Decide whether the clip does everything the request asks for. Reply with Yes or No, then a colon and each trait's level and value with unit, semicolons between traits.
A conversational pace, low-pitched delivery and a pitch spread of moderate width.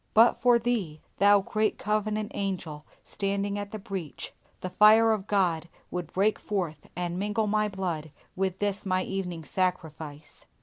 No: average, 150 wpm; high, 195 Hz; average, 3.1 semitones